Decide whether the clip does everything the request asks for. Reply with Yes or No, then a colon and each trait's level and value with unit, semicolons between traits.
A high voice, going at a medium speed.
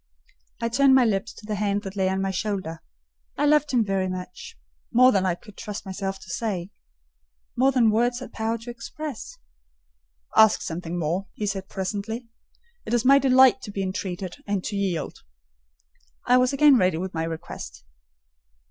Yes: high, 200 Hz; average, 170 wpm